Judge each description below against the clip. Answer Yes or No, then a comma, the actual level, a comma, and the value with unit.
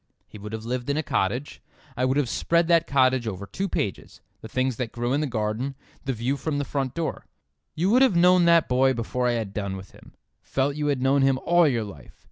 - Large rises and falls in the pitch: No, average, 4.2 semitones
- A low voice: Yes, low, 130 Hz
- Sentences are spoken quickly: Yes, fast, 235 wpm